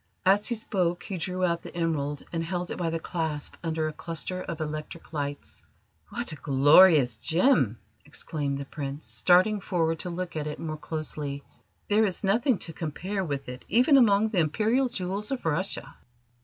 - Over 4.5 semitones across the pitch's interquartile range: No, average, 4.2 semitones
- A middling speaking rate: Yes, average, 180 wpm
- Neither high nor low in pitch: Yes, medium, 170 Hz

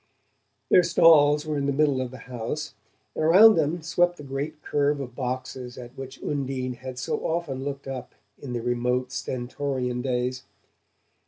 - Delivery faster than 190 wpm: No, average, 165 wpm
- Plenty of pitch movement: No, average, 2.8 semitones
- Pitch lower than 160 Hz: Yes, low, 135 Hz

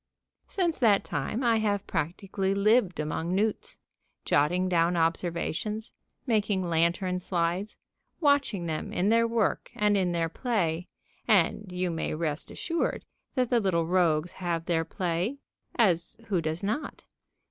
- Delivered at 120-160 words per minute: Yes, slow, 135 wpm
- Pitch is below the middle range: No, medium, 185 Hz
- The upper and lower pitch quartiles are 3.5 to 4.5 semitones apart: Yes, average, 4.2 semitones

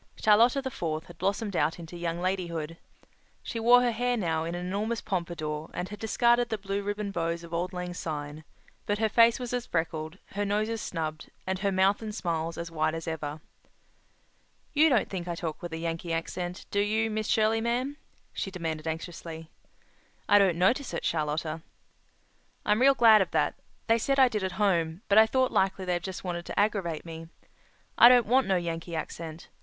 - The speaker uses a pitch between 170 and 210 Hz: Yes, medium, 185 Hz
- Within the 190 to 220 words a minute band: Yes, average, 195 wpm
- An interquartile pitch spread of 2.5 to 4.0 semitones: No, average, 4.7 semitones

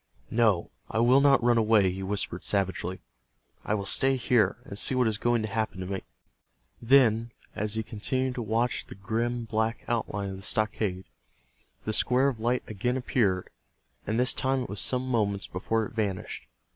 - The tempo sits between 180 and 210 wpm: Yes, average, 185 wpm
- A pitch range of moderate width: Yes, average, 3.4 semitones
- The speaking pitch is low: Yes, low, 110 Hz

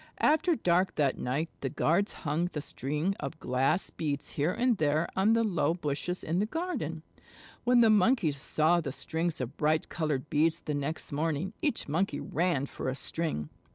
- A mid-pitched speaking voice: Yes, medium, 160 Hz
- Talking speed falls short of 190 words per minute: Yes, average, 180 wpm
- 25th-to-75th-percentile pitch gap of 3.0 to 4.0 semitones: No, average, 4.6 semitones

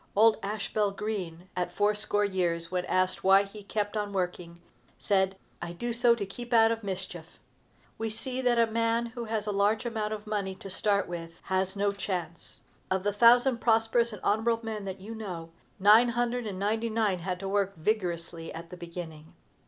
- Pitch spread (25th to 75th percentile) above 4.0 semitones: No, average, 3.3 semitones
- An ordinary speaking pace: Yes, average, 190 wpm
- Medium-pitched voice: No, high, 205 Hz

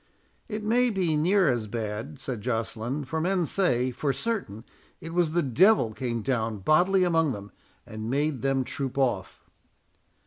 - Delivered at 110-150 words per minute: No, average, 160 wpm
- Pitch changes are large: Yes, wide, 6.9 semitones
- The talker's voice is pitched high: No, low, 135 Hz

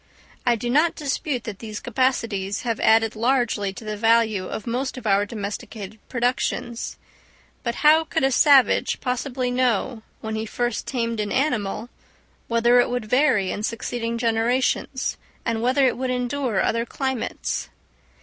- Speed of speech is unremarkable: Yes, average, 150 wpm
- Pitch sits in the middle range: No, high, 235 Hz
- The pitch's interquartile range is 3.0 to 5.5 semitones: No, narrow, 2.6 semitones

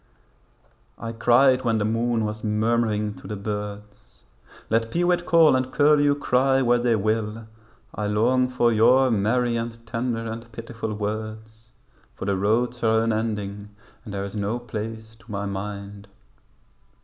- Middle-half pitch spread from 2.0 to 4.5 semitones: Yes, narrow, 2.4 semitones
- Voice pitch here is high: No, low, 115 Hz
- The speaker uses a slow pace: No, average, 150 wpm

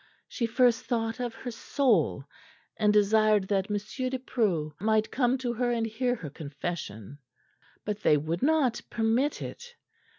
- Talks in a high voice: Yes, high, 225 Hz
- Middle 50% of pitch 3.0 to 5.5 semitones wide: Yes, average, 4.0 semitones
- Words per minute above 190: No, average, 155 wpm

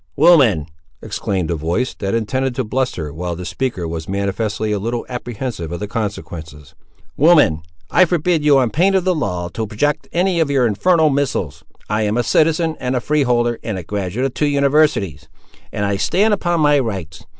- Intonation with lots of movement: Yes, wide, 7.4 semitones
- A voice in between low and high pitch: No, low, 120 Hz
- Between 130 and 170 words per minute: No, average, 185 wpm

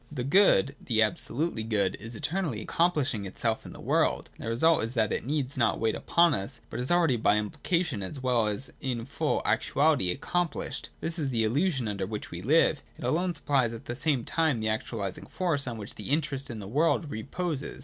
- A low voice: Yes, low, 130 Hz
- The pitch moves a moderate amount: No, wide, 5.9 semitones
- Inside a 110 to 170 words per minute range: No, fast, 205 wpm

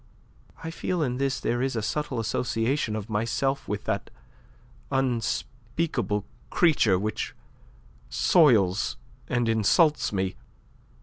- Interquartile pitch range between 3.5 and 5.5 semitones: Yes, average, 4.3 semitones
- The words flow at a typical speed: No, slow, 115 wpm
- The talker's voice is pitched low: Yes, low, 120 Hz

